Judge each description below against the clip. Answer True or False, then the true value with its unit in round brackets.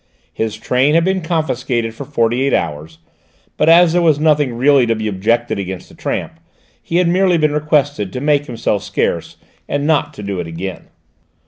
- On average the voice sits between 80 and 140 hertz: True (135 Hz)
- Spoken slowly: False (190 wpm)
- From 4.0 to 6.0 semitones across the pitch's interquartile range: True (5.6 semitones)